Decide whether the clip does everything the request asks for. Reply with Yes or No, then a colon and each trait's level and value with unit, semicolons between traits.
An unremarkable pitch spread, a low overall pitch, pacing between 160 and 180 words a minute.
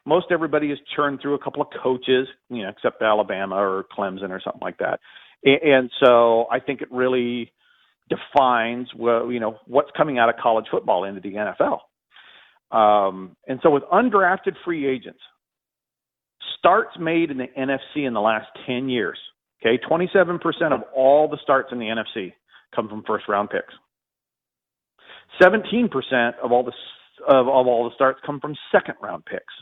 Yes: average, 4.0 semitones; low, 130 Hz; average, 165 wpm